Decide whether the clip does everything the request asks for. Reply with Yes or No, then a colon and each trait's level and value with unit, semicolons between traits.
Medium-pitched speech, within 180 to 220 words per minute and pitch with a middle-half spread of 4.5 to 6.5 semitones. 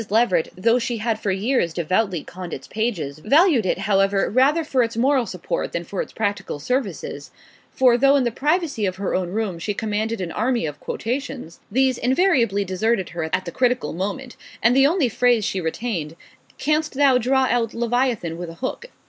No: high, 225 Hz; average, 190 wpm; wide, 5.5 semitones